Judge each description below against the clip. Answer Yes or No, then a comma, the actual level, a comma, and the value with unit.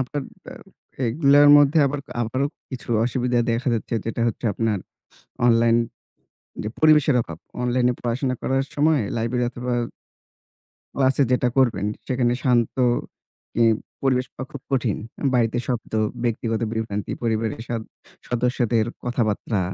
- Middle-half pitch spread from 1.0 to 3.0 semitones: Yes, narrow, 2.4 semitones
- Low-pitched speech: Yes, low, 125 Hz